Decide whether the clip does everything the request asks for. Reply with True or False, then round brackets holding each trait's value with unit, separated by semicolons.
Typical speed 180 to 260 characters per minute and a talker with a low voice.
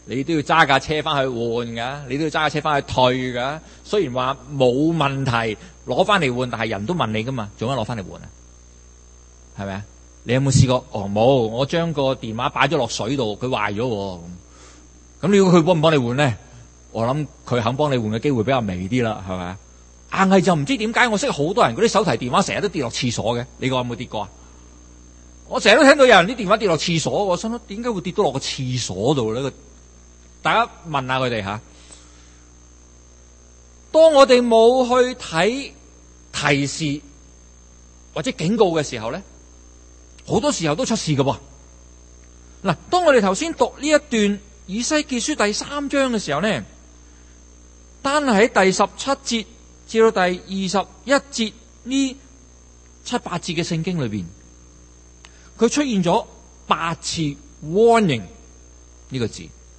True (250 characters per minute; 130 Hz)